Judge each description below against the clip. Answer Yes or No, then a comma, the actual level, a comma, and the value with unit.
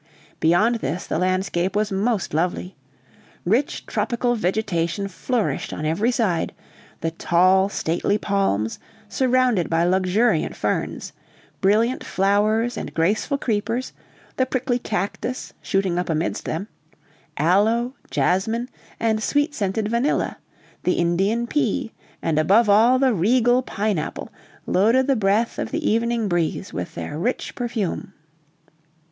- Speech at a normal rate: No, slow, 125 wpm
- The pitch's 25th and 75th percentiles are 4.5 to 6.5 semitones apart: Yes, average, 4.8 semitones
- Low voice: No, high, 205 Hz